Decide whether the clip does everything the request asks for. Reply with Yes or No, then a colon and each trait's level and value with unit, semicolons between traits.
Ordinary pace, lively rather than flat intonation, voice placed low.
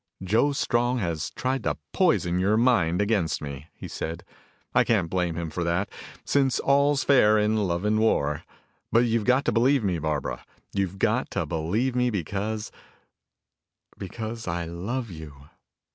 Yes: average, 160 wpm; wide, 5.7 semitones; low, 105 Hz